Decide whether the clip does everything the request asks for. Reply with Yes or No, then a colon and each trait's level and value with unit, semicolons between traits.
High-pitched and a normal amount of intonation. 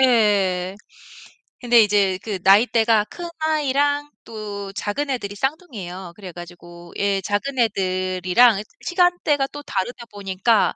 No: high, 210 Hz; wide, 5.7 semitones